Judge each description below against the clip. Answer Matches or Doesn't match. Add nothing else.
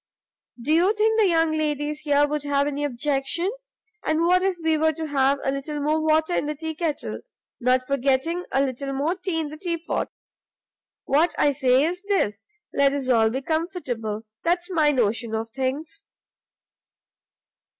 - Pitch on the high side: Matches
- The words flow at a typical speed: Matches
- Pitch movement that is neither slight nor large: Matches